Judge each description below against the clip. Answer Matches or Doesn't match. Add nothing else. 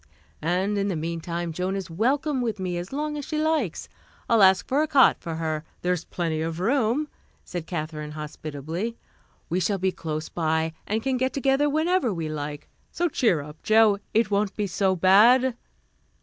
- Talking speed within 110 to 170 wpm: Doesn't match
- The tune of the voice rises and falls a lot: Matches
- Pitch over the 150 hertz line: Matches